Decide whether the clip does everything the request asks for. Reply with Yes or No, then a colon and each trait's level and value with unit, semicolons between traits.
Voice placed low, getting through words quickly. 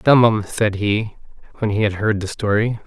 Yes: low, 105 Hz; fast, 210 wpm